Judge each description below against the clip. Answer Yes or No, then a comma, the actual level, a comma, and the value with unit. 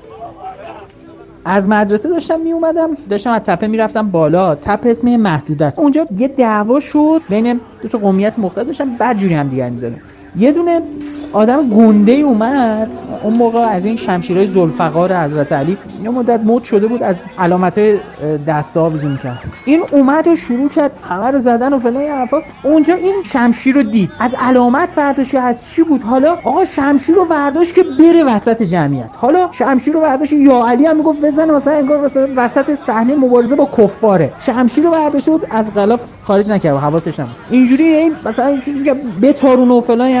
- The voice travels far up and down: Yes, wide, 6.0 semitones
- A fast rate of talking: Yes, fast, 170 wpm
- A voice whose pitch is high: Yes, high, 245 Hz